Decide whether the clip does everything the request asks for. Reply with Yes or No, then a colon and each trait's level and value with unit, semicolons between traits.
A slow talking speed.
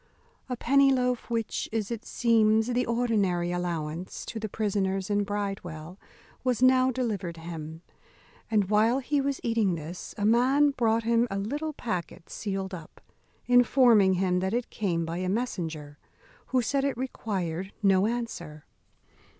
No: average, 150 wpm